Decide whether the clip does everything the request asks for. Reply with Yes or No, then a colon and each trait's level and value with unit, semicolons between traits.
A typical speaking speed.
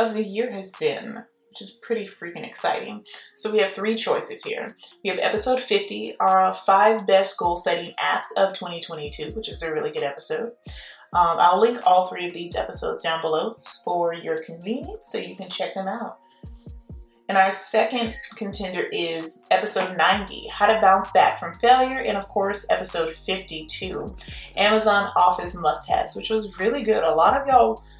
Yes: average, 180 wpm